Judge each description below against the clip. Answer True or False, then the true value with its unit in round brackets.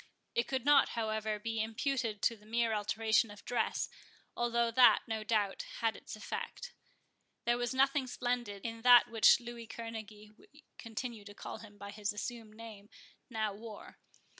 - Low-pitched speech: False (225 Hz)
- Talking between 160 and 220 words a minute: True (165 wpm)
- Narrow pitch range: True (2.1 semitones)